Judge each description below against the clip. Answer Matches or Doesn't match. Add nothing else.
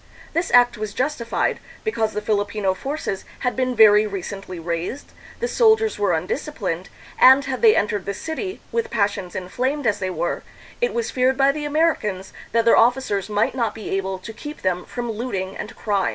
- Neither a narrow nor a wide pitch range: Doesn't match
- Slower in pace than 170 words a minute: Doesn't match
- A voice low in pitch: Doesn't match